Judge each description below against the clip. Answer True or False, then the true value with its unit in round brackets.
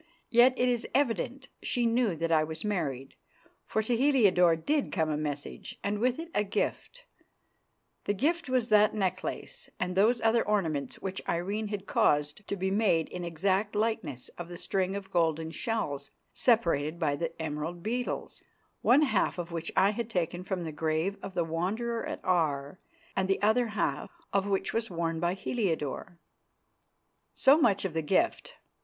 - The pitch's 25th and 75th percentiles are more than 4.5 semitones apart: True (5.6 semitones)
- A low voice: False (190 Hz)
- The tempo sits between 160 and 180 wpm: True (170 wpm)